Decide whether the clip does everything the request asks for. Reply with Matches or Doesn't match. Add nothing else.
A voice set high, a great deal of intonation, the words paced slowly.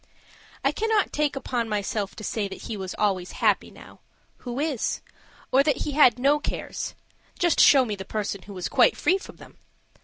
Doesn't match